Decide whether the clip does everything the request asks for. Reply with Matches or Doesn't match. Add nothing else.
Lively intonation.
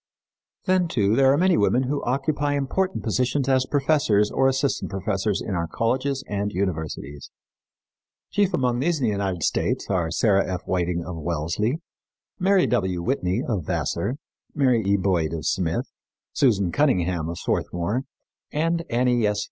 Matches